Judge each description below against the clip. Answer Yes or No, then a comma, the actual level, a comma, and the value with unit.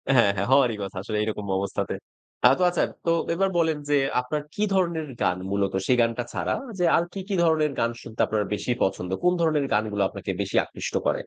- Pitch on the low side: Yes, low, 125 Hz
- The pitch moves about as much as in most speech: No, wide, 7.6 semitones